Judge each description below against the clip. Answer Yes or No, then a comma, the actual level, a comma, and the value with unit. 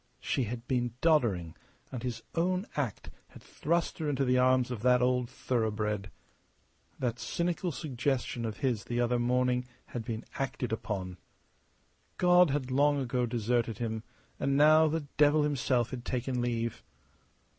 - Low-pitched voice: Yes, low, 125 Hz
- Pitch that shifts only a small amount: No, average, 3.3 semitones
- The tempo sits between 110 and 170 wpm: Yes, average, 150 wpm